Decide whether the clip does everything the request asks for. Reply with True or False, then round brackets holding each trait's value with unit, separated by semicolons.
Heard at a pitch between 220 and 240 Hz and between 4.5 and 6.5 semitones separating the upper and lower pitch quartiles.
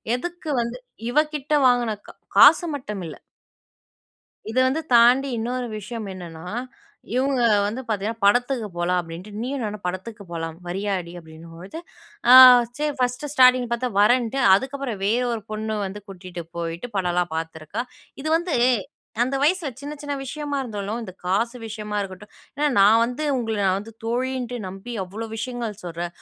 True (225 Hz; 5.2 semitones)